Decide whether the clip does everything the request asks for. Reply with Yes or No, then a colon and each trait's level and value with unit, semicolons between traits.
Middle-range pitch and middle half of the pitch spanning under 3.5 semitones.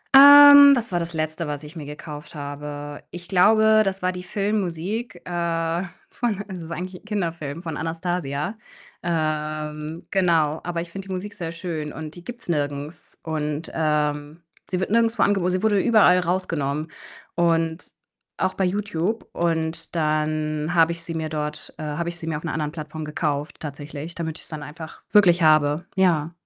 Yes: medium, 165 Hz; average, 3.1 semitones